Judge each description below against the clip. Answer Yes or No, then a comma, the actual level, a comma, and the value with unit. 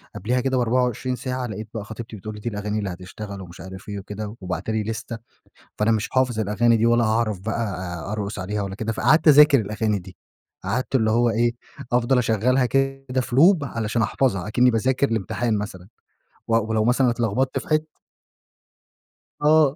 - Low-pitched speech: Yes, low, 115 Hz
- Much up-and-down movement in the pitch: No, average, 3.3 semitones